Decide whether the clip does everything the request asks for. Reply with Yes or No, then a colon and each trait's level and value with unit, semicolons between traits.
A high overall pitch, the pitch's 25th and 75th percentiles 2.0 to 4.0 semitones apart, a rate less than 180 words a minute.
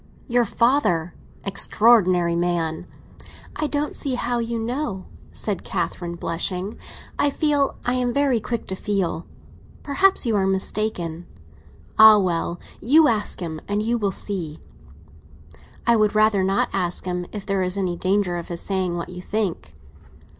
No: high, 200 Hz; average, 4.9 semitones; average, 150 wpm